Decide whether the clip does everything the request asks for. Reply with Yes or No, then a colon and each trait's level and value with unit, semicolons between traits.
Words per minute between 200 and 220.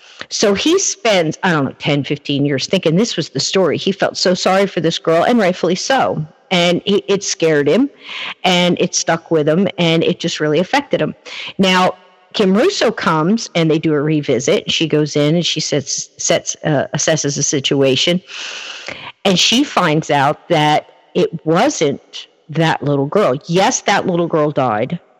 No: average, 180 wpm